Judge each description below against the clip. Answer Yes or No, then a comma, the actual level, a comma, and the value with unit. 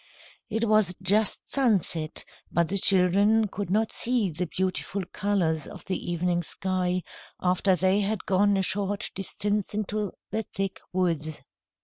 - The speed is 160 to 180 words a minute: No, average, 140 wpm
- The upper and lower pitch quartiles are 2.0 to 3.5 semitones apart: Yes, narrow, 2.4 semitones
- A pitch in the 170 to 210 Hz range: Yes, high, 190 Hz